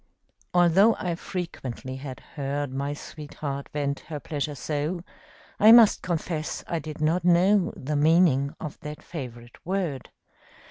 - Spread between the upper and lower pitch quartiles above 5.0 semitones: No, average, 3.7 semitones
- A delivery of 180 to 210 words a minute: No, slow, 135 wpm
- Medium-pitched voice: Yes, medium, 155 Hz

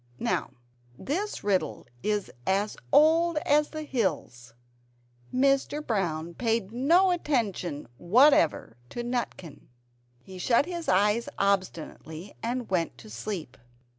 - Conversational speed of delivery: No, slow, 110 wpm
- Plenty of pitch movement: Yes, wide, 8.1 semitones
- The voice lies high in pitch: Yes, high, 215 Hz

